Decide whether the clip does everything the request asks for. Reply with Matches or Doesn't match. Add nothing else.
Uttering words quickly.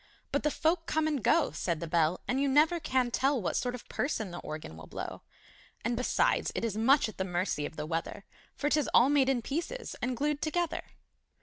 Matches